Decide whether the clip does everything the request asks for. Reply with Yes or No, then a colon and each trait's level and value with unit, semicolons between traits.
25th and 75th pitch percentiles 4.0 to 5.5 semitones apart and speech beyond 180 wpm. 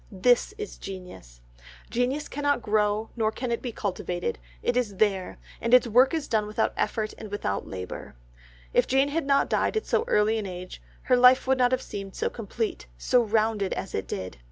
Yes: average, 4.3 semitones; average, 195 wpm